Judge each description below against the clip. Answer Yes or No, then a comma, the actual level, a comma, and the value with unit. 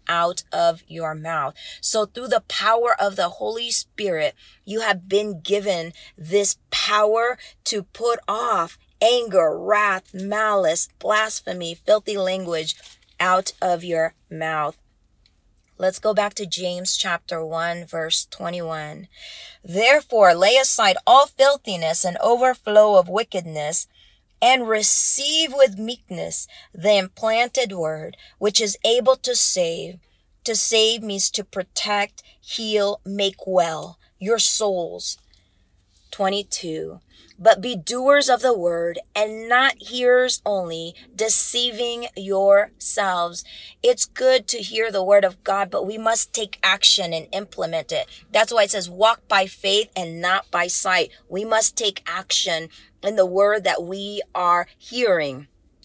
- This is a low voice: No, high, 200 Hz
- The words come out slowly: Yes, slow, 130 wpm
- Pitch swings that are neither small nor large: Yes, average, 4.8 semitones